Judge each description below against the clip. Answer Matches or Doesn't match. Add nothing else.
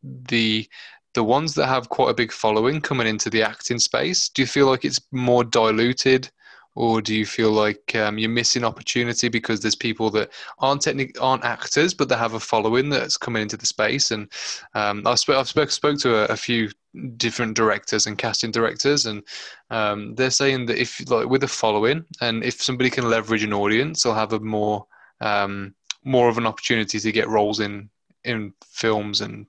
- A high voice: Doesn't match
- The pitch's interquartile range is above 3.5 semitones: Doesn't match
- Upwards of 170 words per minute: Matches